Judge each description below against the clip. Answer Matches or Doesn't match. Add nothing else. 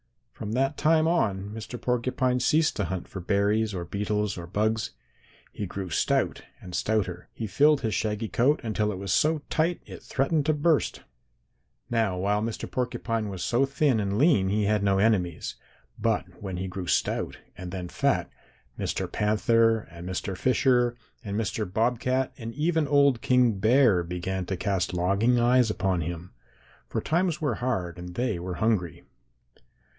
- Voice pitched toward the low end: Matches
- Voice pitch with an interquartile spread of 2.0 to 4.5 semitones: Doesn't match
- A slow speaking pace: Doesn't match